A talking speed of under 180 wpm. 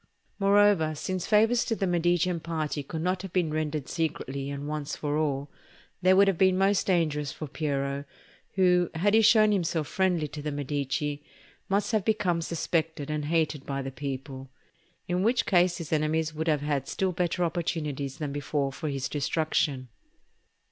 Yes: average, 170 wpm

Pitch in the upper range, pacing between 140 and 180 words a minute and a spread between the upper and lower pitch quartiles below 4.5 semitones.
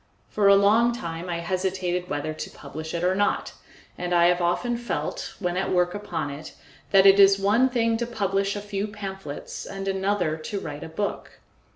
No: high, 195 Hz; average, 195 wpm; average, 2.9 semitones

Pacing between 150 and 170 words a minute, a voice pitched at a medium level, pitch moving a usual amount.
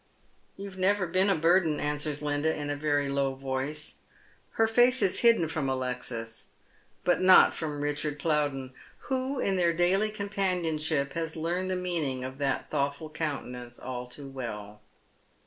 Yes: average, 160 wpm; medium, 150 Hz; average, 4.9 semitones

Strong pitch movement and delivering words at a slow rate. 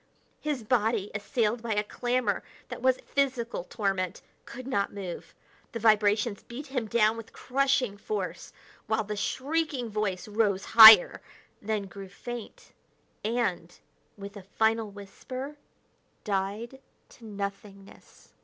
No: average, 3.3 semitones; slow, 125 wpm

